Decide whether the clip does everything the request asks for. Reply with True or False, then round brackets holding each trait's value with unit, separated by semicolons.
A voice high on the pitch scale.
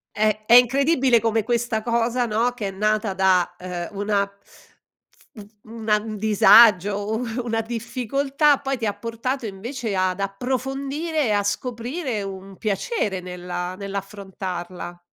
True (215 Hz)